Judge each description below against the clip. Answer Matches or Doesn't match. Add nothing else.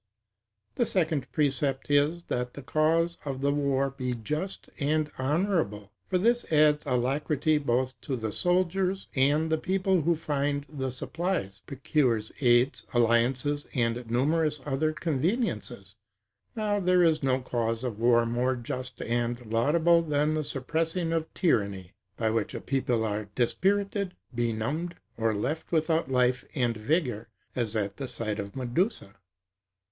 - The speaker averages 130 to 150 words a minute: Matches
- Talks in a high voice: Doesn't match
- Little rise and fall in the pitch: Doesn't match